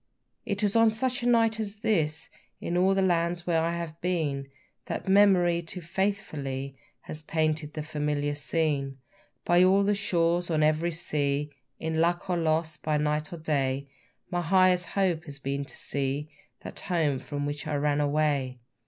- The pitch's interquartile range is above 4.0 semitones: No, average, 3.5 semitones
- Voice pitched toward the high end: No, medium, 160 Hz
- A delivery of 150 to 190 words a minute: Yes, average, 170 wpm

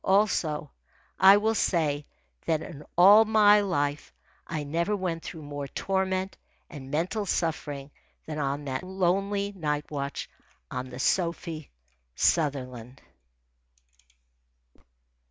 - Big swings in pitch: No, average, 4.9 semitones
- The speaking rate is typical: No, slow, 110 wpm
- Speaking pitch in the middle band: Yes, medium, 165 Hz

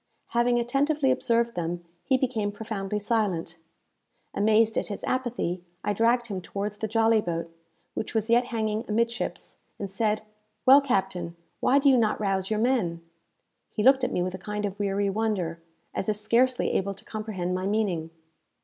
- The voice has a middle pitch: No, high, 215 Hz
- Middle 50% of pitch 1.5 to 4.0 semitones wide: Yes, average, 3.5 semitones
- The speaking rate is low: No, average, 175 wpm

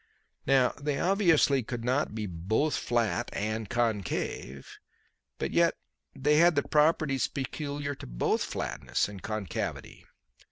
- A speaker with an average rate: No, slow, 125 wpm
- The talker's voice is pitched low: Yes, low, 130 Hz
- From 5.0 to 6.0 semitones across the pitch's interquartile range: Yes, wide, 5.4 semitones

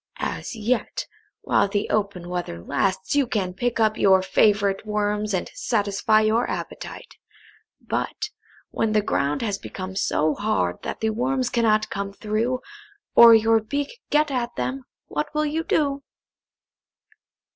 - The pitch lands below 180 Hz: No, high, 215 Hz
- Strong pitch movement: No, average, 3.4 semitones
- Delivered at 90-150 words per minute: Yes, average, 145 wpm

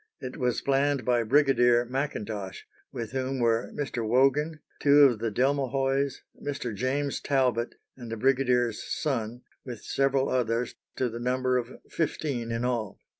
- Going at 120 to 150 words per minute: Yes, average, 145 wpm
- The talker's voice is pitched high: No, low, 125 Hz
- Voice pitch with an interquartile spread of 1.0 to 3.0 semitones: Yes, narrow, 2.6 semitones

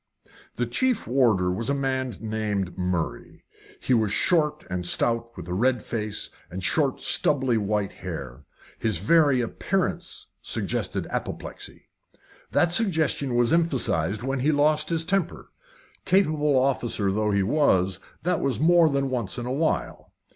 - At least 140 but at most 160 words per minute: Yes, average, 145 wpm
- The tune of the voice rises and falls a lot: Yes, wide, 6.7 semitones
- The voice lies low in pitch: Yes, low, 125 Hz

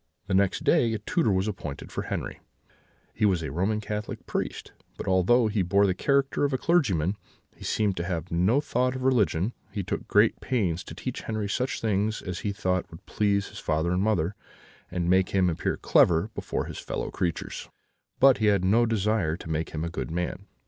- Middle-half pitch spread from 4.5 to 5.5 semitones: No, average, 3.8 semitones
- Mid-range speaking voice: No, low, 100 Hz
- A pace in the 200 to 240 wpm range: Yes, fast, 205 wpm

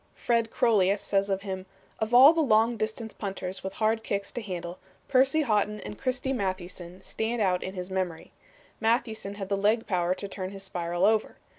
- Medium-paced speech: Yes, average, 185 wpm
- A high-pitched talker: Yes, high, 205 Hz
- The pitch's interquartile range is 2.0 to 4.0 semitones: Yes, average, 3.1 semitones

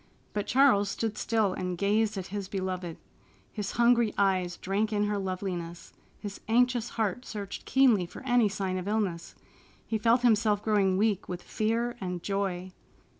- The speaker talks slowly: No, average, 160 wpm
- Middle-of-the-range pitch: No, high, 205 Hz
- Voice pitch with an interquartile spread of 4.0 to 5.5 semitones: No, average, 3.0 semitones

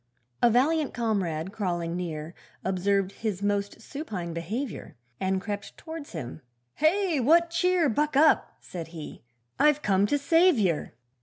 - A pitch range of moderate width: No, wide, 8.7 semitones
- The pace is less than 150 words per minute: Yes, average, 140 wpm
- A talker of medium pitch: No, high, 210 Hz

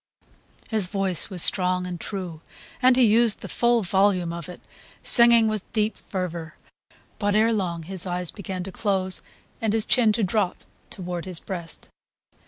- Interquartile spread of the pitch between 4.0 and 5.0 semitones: No, average, 3.3 semitones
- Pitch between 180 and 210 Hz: Yes, high, 190 Hz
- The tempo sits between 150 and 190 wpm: Yes, average, 165 wpm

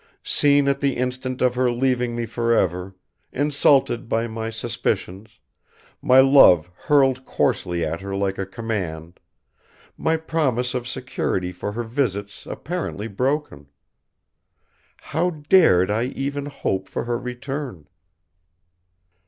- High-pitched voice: No, low, 120 Hz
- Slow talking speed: Yes, slow, 120 wpm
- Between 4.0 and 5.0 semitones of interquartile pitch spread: No, wide, 5.6 semitones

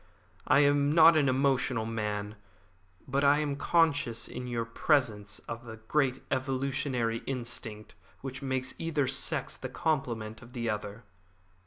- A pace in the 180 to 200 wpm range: No, average, 140 wpm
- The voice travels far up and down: No, average, 3.7 semitones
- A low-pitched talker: Yes, low, 130 Hz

